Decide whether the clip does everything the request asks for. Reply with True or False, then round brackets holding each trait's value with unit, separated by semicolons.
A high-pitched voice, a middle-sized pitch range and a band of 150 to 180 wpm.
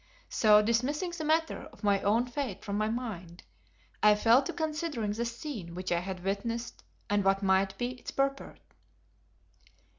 True (225 Hz; 4.9 semitones; 160 wpm)